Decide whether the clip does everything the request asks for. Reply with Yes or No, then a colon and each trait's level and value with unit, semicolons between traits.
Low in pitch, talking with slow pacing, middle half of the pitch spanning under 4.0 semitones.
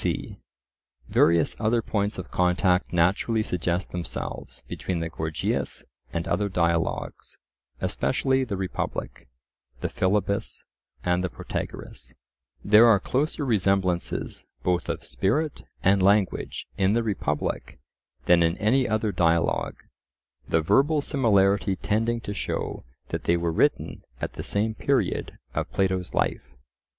Yes: very low, 95 Hz; slow, 125 wpm; average, 3.6 semitones